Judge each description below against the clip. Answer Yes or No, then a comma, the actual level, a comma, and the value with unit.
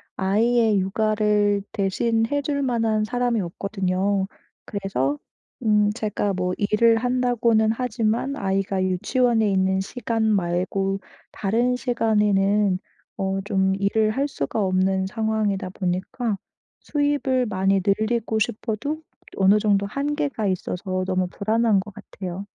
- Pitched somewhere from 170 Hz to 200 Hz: No, high, 210 Hz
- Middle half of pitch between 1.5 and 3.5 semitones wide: Yes, average, 3.0 semitones